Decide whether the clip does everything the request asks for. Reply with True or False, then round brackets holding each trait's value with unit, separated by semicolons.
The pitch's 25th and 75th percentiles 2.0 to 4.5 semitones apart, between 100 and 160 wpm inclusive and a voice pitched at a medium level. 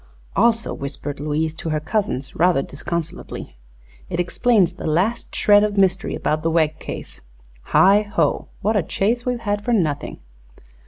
False (5.1 semitones; 155 wpm; 180 Hz)